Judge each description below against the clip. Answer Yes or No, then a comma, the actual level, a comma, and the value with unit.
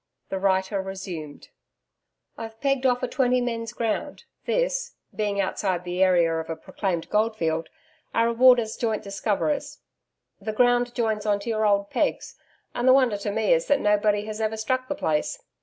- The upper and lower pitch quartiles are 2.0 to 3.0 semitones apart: No, average, 4.0 semitones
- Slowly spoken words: No, average, 175 wpm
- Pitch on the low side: No, high, 215 Hz